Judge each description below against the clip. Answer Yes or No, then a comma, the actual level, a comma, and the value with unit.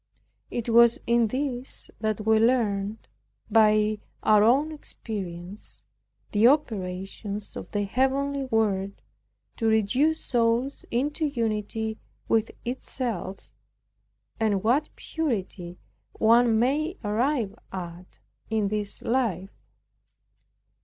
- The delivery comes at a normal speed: No, slow, 100 wpm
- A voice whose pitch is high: Yes, high, 225 Hz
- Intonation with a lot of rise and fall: No, average, 3.6 semitones